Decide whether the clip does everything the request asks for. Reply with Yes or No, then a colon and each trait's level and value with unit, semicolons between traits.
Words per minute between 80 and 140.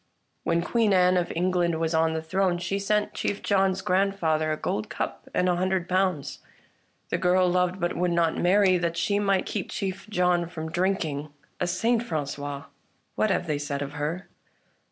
No: average, 180 wpm